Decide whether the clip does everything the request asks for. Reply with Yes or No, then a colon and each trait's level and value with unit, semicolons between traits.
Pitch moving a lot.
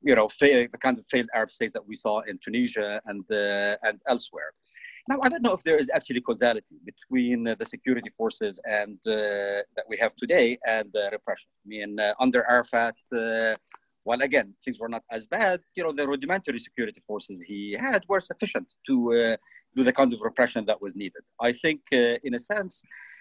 Yes: wide, 6.8 semitones